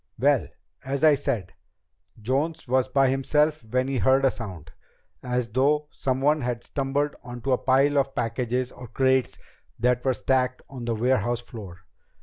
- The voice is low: Yes, low, 130 Hz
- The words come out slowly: No, average, 155 wpm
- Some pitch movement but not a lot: No, narrow, 2.2 semitones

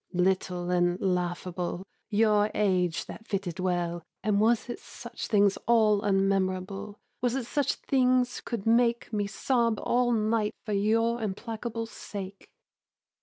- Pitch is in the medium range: No, high, 210 Hz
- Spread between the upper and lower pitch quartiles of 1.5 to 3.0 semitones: No, average, 3.6 semitones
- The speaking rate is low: Yes, slow, 130 wpm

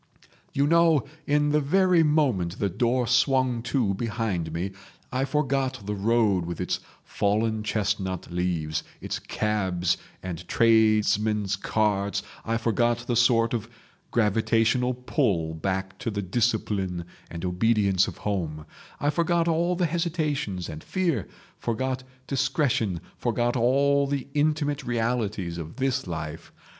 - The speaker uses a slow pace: Yes, slow, 130 wpm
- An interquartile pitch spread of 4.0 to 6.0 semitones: Yes, wide, 5.6 semitones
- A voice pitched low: Yes, low, 115 Hz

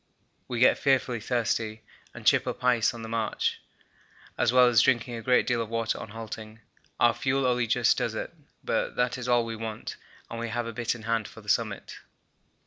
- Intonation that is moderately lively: No, narrow, 1.7 semitones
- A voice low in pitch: Yes, low, 115 Hz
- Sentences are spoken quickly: Yes, fast, 210 wpm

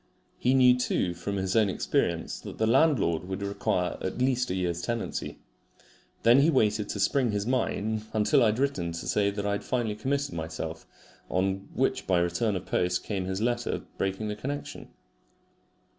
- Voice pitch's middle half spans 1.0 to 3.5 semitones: No, average, 4.6 semitones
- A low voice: Yes, low, 105 Hz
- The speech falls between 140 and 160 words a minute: No, average, 180 wpm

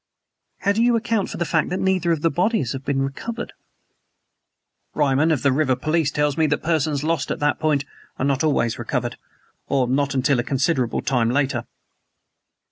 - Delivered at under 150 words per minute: No, average, 190 wpm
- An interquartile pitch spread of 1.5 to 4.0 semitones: Yes, average, 3.6 semitones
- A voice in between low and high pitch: Yes, medium, 145 Hz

